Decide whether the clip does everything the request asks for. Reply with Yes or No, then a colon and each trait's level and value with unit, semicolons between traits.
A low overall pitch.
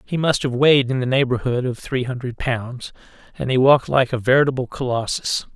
Yes: low, 130 Hz